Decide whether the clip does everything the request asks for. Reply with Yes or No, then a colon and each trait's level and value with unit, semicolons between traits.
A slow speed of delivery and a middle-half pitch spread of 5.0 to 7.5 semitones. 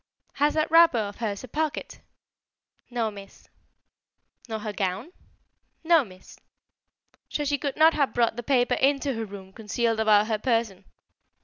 No: average, 150 wpm; average, 5.3 semitones